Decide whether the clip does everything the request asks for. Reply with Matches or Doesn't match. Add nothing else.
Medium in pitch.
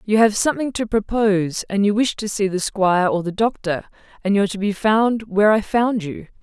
Doesn't match